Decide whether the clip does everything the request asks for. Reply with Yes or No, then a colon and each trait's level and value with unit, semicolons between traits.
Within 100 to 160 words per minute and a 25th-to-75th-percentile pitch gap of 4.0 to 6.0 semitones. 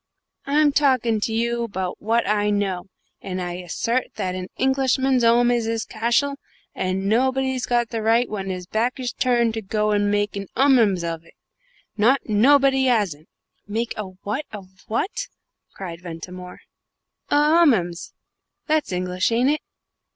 Yes: average, 150 wpm; average, 5.0 semitones